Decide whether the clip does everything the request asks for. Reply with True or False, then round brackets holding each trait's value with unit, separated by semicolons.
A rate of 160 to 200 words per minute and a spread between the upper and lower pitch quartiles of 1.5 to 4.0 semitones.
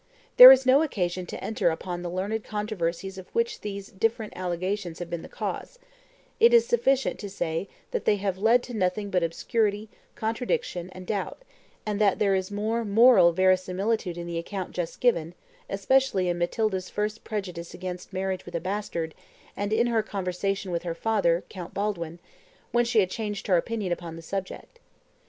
True (180 wpm; 3.6 semitones)